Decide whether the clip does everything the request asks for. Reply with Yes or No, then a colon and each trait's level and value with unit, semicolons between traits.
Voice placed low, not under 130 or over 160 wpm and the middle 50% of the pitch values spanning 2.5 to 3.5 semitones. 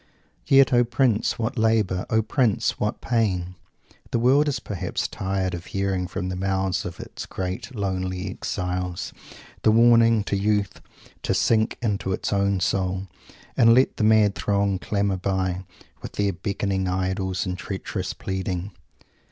Yes: low, 100 Hz; average, 150 wpm; average, 2.9 semitones